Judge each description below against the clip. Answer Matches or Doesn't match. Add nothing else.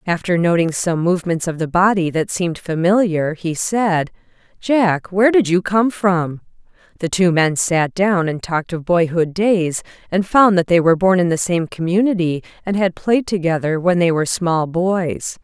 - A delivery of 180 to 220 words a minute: Matches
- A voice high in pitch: Doesn't match